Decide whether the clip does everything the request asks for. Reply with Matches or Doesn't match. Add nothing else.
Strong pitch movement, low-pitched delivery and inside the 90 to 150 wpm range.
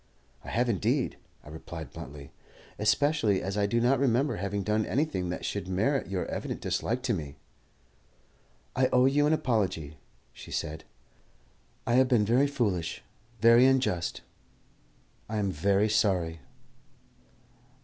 Matches